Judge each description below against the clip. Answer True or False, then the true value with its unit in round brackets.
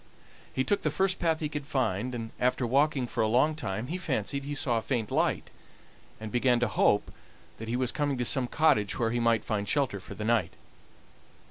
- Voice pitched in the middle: False (125 Hz)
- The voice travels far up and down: False (4.3 semitones)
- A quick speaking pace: True (215 wpm)